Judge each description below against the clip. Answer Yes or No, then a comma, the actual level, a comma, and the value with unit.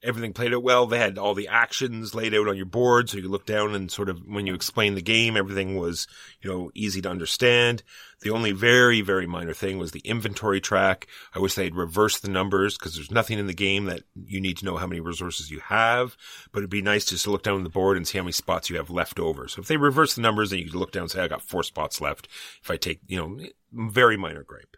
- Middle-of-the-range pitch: No, low, 100 Hz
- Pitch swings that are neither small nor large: Yes, average, 3.1 semitones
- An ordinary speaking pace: No, fast, 270 wpm